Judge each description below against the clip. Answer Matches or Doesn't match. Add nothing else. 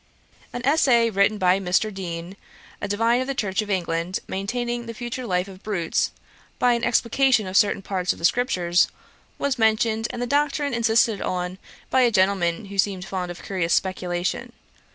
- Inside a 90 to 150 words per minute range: Doesn't match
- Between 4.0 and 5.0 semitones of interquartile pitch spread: Matches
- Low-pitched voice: Doesn't match